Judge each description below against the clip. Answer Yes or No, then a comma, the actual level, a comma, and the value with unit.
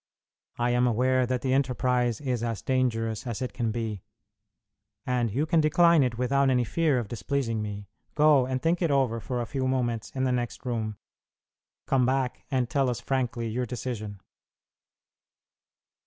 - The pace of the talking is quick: No, average, 170 wpm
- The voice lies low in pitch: Yes, low, 125 Hz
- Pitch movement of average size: No, narrow, 2.3 semitones